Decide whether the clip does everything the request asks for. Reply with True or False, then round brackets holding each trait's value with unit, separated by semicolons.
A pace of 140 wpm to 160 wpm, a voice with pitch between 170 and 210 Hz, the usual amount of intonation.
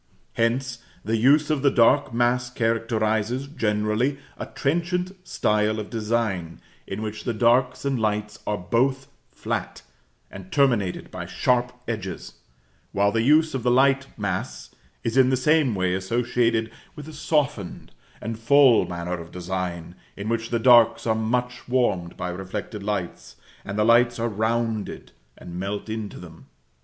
False (150 wpm; 115 Hz; 3.4 semitones)